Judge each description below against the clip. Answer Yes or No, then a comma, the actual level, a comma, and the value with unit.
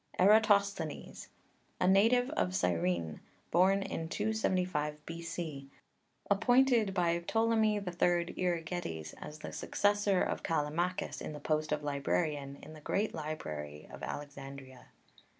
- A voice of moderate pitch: Yes, medium, 165 Hz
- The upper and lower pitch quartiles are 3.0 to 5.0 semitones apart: No, wide, 5.6 semitones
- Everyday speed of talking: No, slow, 115 wpm